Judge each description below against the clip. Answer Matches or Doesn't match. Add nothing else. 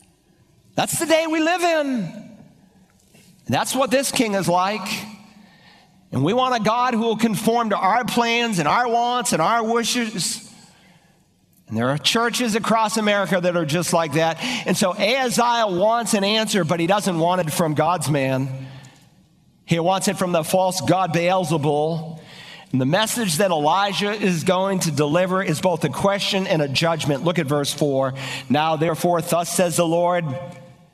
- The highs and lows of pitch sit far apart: Doesn't match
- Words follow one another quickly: Doesn't match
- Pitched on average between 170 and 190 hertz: Matches